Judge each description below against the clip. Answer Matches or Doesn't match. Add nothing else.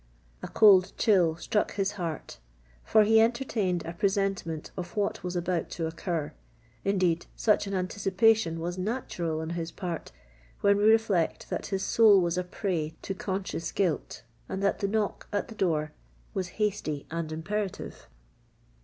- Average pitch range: Matches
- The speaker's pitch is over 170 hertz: Matches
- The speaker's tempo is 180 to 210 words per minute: Doesn't match